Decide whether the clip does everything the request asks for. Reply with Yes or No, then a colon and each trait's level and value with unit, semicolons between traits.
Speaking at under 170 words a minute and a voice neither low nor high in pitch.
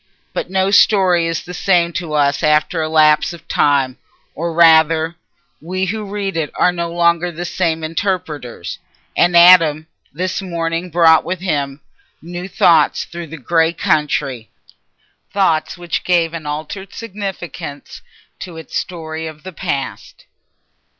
Yes: slow, 135 wpm; medium, 165 Hz